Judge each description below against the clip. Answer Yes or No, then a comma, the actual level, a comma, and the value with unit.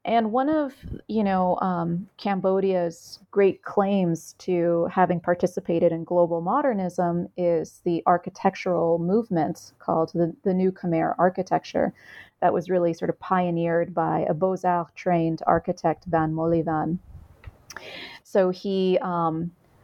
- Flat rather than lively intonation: Yes, narrow, 2.0 semitones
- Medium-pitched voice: Yes, medium, 175 Hz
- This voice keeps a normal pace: No, slow, 120 wpm